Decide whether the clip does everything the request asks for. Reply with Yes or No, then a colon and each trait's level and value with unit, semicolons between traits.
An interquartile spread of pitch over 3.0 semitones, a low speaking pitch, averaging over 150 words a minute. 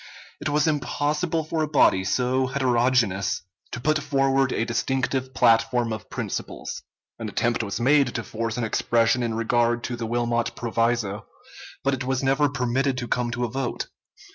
No: narrow, 2.5 semitones; low, 125 Hz; average, 165 wpm